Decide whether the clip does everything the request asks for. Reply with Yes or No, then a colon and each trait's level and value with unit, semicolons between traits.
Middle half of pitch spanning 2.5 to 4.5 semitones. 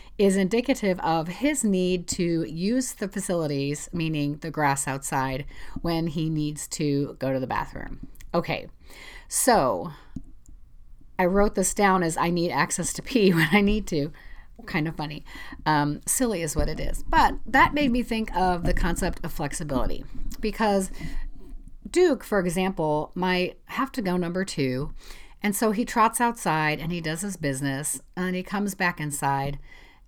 No: average, 5.1 semitones